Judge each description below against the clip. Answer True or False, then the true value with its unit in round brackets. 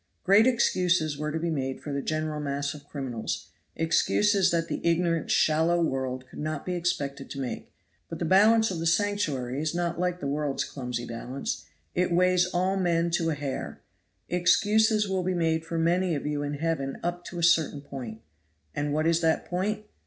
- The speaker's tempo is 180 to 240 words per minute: True (190 wpm)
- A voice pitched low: False (165 Hz)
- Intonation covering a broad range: False (3.8 semitones)